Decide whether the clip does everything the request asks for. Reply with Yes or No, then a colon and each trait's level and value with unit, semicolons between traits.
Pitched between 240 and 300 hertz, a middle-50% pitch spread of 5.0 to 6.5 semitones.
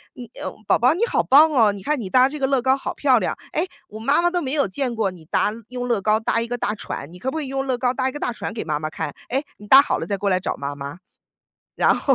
Yes: high, 245 Hz; average, 5.3 semitones